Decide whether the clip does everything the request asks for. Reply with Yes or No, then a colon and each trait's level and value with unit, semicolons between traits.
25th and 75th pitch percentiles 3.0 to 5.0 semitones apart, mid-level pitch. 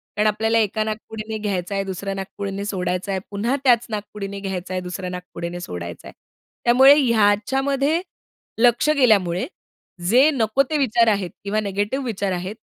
No: average, 3.3 semitones; high, 210 Hz